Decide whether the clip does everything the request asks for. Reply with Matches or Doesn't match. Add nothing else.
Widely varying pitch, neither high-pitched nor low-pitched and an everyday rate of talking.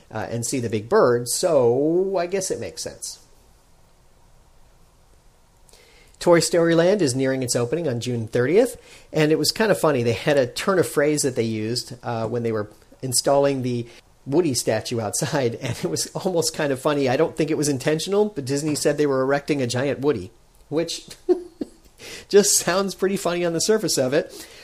Matches